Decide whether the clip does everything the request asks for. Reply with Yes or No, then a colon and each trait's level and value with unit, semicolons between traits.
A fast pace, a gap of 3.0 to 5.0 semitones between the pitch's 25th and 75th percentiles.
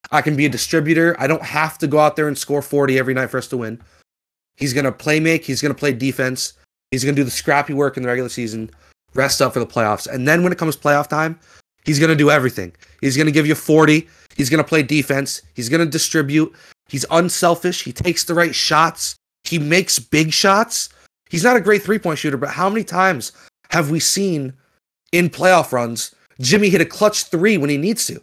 Yes: fast, 235 wpm; average, 3.9 semitones